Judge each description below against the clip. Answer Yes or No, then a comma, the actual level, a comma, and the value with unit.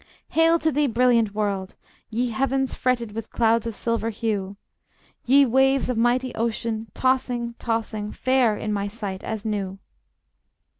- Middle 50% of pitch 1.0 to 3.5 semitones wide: Yes, average, 3.0 semitones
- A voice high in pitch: Yes, high, 230 Hz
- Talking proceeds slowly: No, average, 145 wpm